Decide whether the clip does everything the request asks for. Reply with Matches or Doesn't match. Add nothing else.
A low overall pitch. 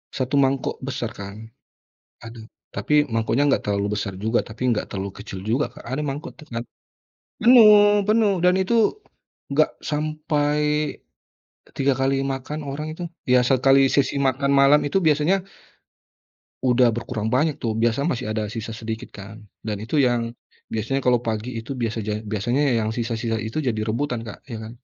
Matches